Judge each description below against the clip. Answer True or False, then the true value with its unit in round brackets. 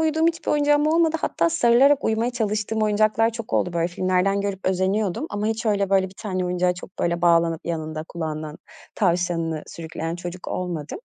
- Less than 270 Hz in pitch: True (190 Hz)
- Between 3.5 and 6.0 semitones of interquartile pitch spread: True (4.6 semitones)